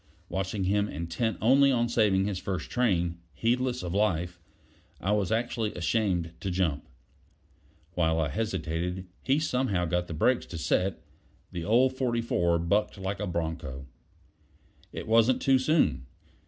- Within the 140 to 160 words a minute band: Yes, average, 145 wpm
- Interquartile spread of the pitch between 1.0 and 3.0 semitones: No, average, 5.1 semitones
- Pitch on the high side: No, low, 100 Hz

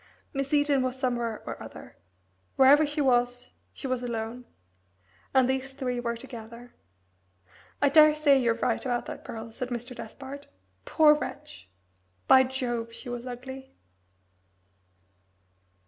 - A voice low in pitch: No, very high, 255 Hz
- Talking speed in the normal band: No, slow, 130 wpm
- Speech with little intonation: Yes, narrow, 2.1 semitones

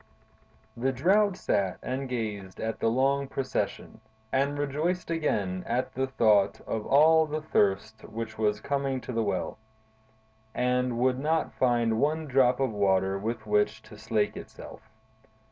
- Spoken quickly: No, average, 145 wpm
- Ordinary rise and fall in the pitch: Yes, average, 4.3 semitones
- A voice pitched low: Yes, low, 125 Hz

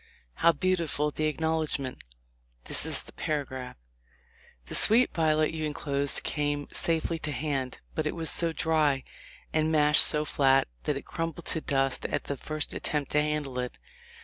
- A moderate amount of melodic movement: No, narrow, 2.3 semitones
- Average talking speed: Yes, average, 170 wpm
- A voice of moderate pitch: Yes, medium, 150 Hz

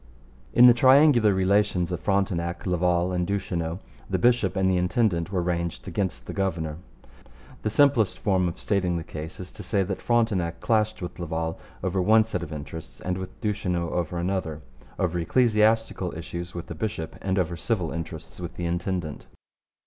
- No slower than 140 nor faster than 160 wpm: No, average, 170 wpm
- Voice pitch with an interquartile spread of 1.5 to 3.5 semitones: Yes, average, 3.1 semitones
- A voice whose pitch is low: Yes, very low, 90 Hz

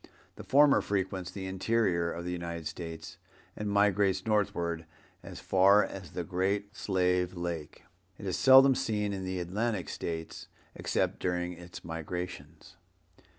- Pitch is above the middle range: No, very low, 95 Hz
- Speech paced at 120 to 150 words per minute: Yes, average, 140 wpm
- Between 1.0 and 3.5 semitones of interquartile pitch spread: Yes, average, 2.7 semitones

